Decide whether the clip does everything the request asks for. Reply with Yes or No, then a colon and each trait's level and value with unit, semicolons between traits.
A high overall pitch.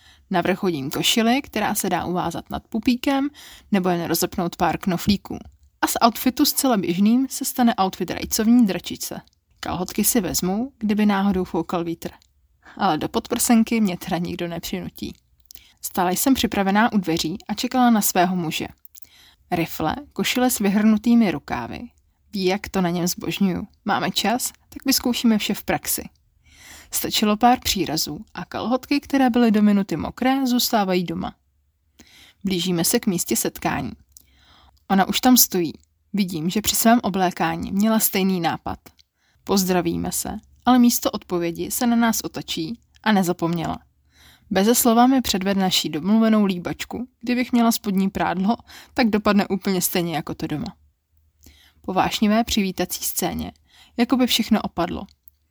Yes: high, 195 Hz